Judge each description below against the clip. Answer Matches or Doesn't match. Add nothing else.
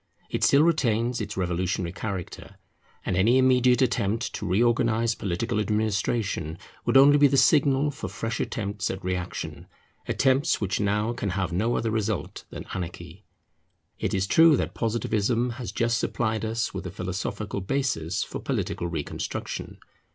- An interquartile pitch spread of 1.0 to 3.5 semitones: Doesn't match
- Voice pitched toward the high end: Doesn't match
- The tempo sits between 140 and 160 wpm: Matches